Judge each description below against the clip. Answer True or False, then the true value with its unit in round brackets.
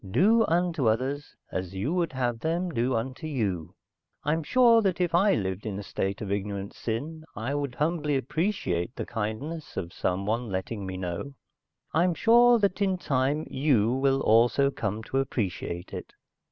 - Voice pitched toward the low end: True (130 Hz)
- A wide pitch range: True (7.8 semitones)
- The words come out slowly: False (165 wpm)